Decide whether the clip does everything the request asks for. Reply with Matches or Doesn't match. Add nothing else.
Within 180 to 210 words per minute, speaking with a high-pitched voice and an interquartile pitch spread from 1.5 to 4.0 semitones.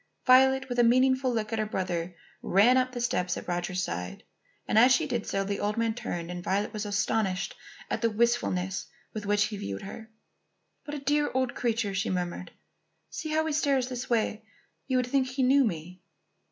Doesn't match